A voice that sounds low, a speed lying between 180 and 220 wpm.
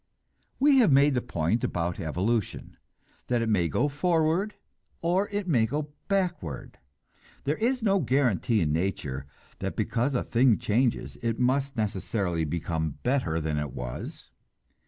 No: low, 120 Hz; average, 145 wpm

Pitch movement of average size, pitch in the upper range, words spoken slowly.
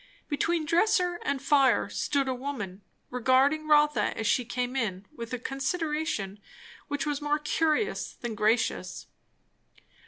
Yes: average, 3.8 semitones; very high, 275 Hz; slow, 130 wpm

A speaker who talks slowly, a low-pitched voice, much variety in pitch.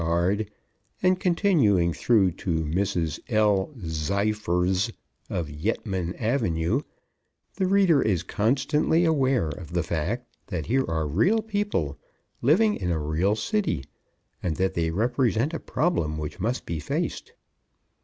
Yes: slow, 130 wpm; low, 100 Hz; wide, 7.9 semitones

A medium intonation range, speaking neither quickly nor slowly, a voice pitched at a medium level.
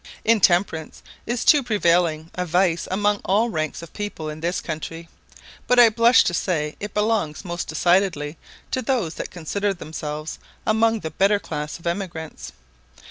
Yes: average, 4.6 semitones; average, 155 wpm; medium, 175 Hz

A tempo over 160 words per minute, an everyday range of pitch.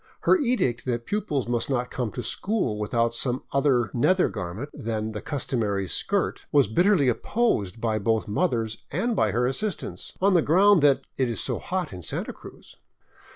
No: average, 185 wpm; wide, 8.2 semitones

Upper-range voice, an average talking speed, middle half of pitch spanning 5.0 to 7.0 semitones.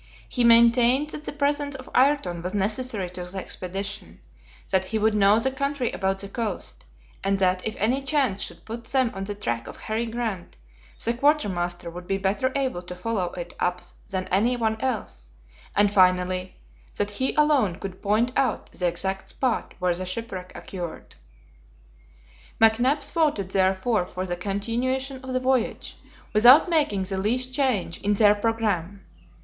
Yes: high, 210 Hz; average, 165 wpm; average, 5.3 semitones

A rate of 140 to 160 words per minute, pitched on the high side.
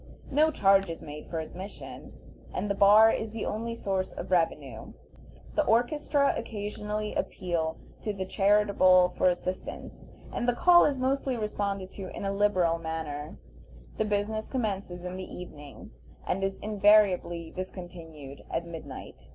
Yes: average, 145 wpm; high, 195 Hz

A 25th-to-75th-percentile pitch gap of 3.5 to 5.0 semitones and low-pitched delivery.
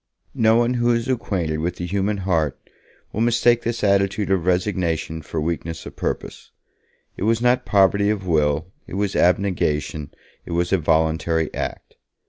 Yes: average, 4.5 semitones; very low, 95 Hz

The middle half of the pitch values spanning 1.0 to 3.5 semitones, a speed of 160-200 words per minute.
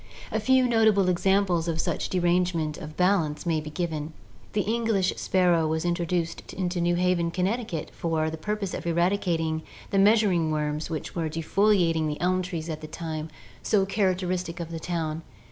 Yes: average, 2.9 semitones; average, 170 wpm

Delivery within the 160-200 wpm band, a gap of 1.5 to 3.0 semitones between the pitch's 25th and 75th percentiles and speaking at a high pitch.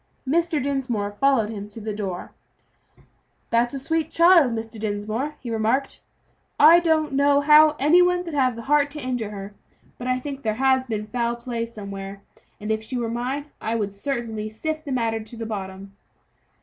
No: average, 185 wpm; average, 4.7 semitones; high, 240 Hz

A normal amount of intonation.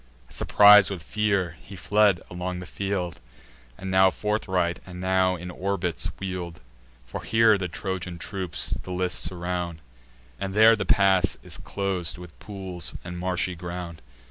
No: narrow, 1.8 semitones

